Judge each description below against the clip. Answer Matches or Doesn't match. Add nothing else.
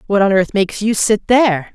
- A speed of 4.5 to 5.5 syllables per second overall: Doesn't match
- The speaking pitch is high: Matches